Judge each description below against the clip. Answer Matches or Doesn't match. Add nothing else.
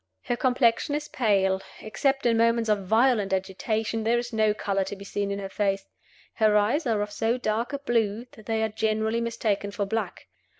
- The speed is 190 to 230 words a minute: Matches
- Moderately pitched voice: Doesn't match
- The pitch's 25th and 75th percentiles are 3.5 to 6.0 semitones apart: Doesn't match